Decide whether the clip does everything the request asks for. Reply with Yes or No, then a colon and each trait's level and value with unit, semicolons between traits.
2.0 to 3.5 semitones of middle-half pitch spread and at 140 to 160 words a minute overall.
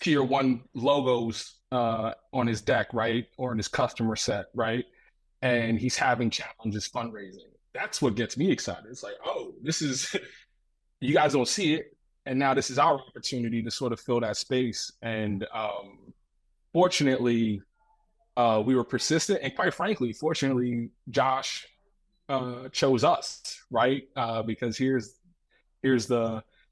Yes: average, 3.2 semitones; average, 150 wpm